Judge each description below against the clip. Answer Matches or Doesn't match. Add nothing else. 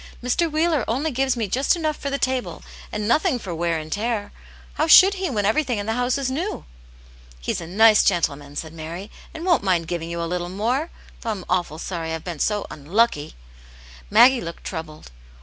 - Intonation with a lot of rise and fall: Matches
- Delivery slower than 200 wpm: Doesn't match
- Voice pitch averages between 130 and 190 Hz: Doesn't match